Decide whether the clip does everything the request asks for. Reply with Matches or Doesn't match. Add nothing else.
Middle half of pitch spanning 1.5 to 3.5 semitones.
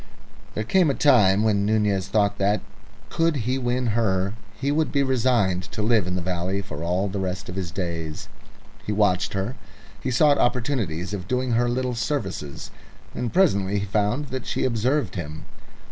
Doesn't match